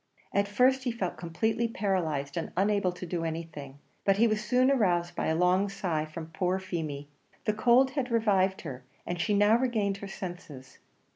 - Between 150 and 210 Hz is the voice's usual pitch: Yes, high, 190 Hz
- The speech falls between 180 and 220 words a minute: Yes, average, 185 wpm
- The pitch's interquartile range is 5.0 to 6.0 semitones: No, average, 4.6 semitones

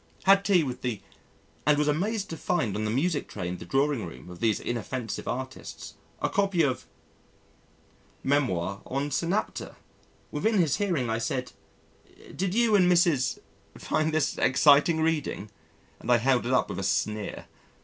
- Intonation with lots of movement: Yes, wide, 6.5 semitones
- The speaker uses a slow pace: No, average, 165 wpm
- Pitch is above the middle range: No, medium, 140 Hz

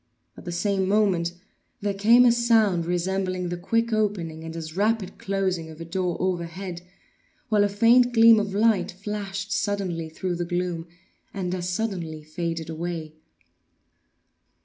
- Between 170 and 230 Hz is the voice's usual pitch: Yes, medium, 185 Hz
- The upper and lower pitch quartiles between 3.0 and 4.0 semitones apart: Yes, average, 3.4 semitones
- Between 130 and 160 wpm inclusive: Yes, average, 150 wpm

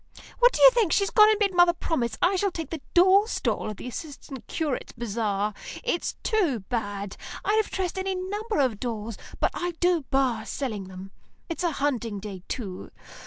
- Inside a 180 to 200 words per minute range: Yes, average, 190 wpm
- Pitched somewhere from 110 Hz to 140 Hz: No, very high, 295 Hz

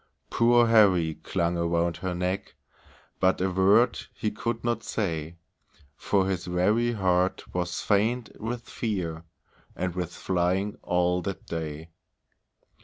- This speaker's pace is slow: Yes, slow, 125 wpm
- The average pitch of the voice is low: Yes, very low, 95 Hz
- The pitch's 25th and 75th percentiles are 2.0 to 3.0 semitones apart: No, average, 3.4 semitones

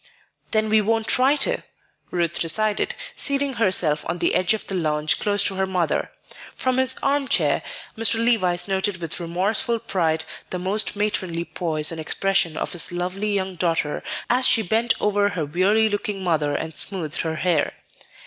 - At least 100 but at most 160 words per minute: No, average, 170 wpm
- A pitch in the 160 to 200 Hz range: Yes, high, 190 Hz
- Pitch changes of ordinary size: Yes, average, 4.4 semitones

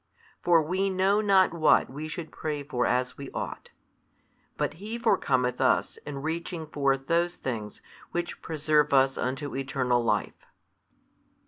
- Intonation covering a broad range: No, average, 4.3 semitones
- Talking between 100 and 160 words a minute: Yes, average, 140 wpm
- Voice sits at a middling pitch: Yes, medium, 150 Hz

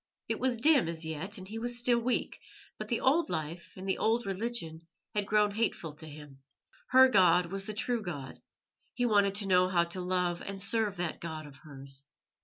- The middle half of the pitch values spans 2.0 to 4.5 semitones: No, average, 5.2 semitones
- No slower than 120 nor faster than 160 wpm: No, fast, 205 wpm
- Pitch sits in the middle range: No, high, 195 Hz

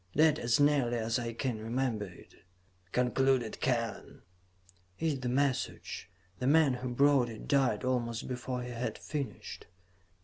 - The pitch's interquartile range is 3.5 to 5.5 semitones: No, narrow, 2.6 semitones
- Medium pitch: No, low, 125 Hz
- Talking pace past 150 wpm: No, average, 145 wpm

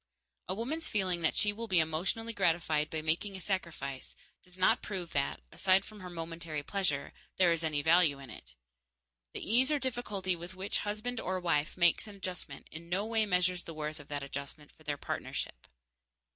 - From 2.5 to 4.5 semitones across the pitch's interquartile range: Yes, average, 4.2 semitones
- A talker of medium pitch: Yes, medium, 180 Hz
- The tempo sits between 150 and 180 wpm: No, average, 190 wpm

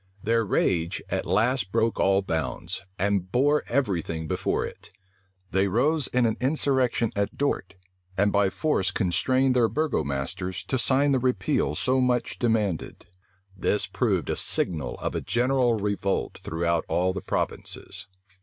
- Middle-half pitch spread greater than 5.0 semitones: Yes, wide, 5.5 semitones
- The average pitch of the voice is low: Yes, low, 105 Hz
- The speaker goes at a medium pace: Yes, average, 145 wpm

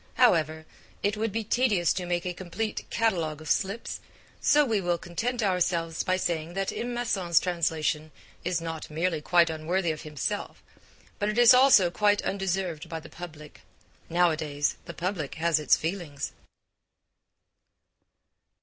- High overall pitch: No, medium, 175 Hz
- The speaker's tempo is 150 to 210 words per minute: No, average, 140 wpm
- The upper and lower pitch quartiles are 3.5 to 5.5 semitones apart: Yes, average, 4.0 semitones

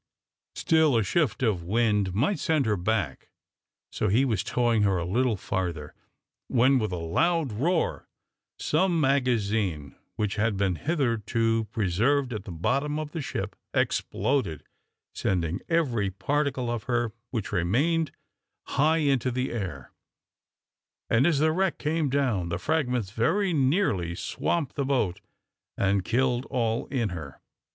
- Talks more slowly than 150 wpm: Yes, average, 140 wpm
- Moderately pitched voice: No, low, 115 Hz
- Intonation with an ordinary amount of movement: No, wide, 6.3 semitones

